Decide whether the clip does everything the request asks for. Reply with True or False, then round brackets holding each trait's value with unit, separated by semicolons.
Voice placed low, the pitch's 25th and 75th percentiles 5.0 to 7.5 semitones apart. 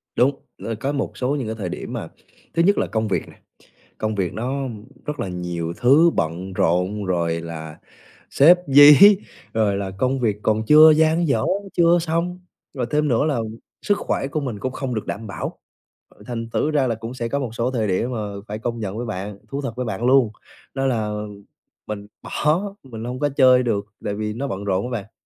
True (120 Hz; 5.3 semitones)